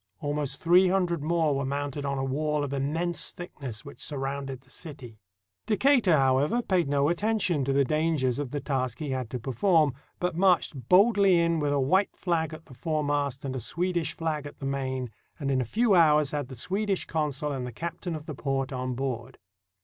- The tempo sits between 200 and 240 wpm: Yes, fast, 205 wpm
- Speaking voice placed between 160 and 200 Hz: No, medium, 145 Hz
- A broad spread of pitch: No, average, 4.0 semitones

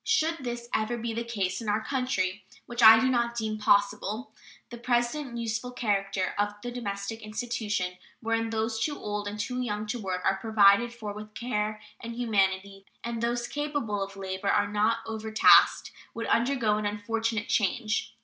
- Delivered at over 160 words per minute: Yes, average, 170 wpm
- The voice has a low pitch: No, high, 220 Hz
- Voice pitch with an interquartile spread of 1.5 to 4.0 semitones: Yes, narrow, 2.5 semitones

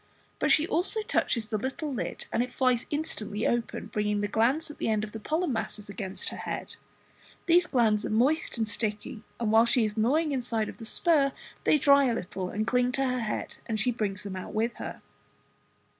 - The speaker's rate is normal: No, fast, 215 wpm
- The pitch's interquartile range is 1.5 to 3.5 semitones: No, average, 4.3 semitones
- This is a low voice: No, high, 235 Hz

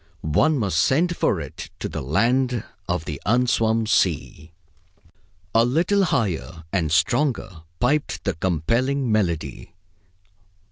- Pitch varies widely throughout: Yes, wide, 7.9 semitones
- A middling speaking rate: No, slow, 120 wpm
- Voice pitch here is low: Yes, low, 110 Hz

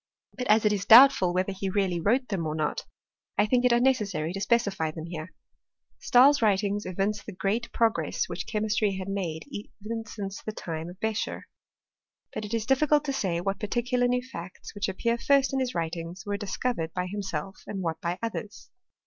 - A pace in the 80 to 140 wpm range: No, average, 190 wpm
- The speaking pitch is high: Yes, high, 205 Hz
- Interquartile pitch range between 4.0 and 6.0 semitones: Yes, average, 4.3 semitones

